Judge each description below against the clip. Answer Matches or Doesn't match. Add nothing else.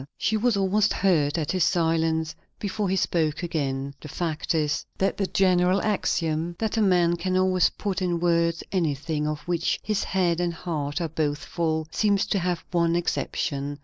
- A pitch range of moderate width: Matches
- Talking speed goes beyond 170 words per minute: Matches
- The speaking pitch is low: Doesn't match